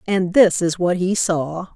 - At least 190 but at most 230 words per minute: Yes, fast, 205 wpm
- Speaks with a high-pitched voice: No, medium, 180 Hz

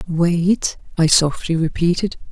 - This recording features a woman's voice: Yes, female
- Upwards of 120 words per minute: No, slow, 105 wpm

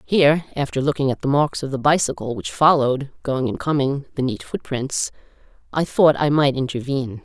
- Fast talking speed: No, average, 180 wpm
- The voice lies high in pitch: No, medium, 140 Hz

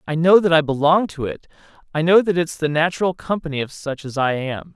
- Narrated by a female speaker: No, male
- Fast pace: Yes, fast, 240 wpm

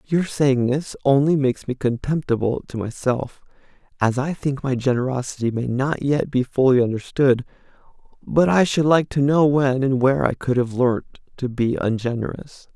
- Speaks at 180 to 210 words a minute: No, average, 170 wpm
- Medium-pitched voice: No, low, 130 Hz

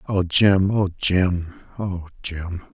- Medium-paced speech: No, slow, 85 wpm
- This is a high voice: No, very low, 90 Hz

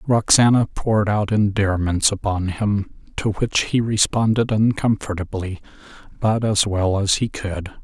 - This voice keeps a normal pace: No, slow, 130 wpm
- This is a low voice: Yes, low, 105 Hz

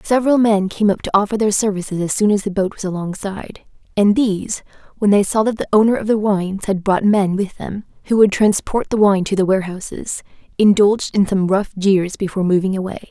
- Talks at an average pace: No, fast, 215 wpm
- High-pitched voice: Yes, high, 200 Hz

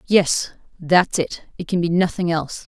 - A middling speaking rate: No, slow, 130 wpm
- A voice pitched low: No, medium, 170 Hz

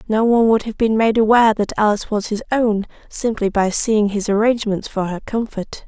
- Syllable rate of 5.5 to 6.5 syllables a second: Yes, 5.6 syllables/s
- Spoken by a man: No, female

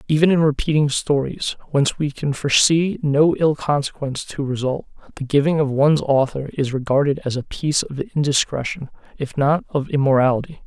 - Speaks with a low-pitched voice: No, medium, 145 Hz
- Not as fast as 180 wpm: Yes, average, 165 wpm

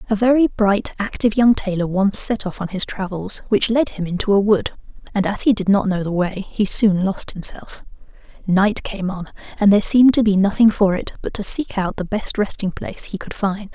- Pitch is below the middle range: No, high, 200 Hz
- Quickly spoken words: Yes, fast, 225 wpm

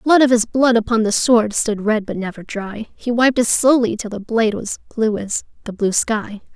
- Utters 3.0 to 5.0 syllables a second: Yes, 4.8 syllables/s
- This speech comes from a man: No, female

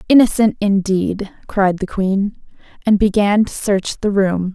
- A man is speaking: No, female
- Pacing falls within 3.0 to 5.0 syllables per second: Yes, 4.0 syllables/s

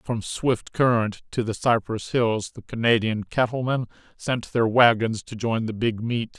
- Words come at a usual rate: Yes, average, 170 wpm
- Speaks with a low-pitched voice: Yes, low, 115 Hz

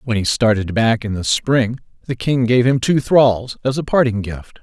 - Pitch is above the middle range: No, low, 120 Hz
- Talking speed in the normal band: No, fast, 220 wpm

